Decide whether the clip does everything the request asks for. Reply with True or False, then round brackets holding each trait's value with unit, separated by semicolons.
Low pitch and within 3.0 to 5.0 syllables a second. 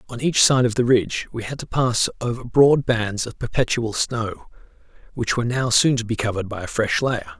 False (120 Hz; 5.4 syllables/s)